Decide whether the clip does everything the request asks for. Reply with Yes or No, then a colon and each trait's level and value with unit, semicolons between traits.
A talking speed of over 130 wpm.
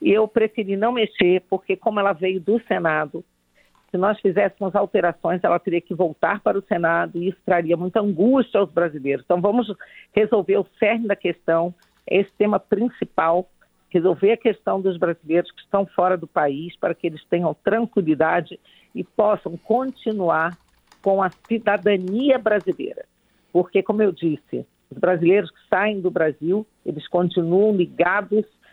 Yes: average, 155 wpm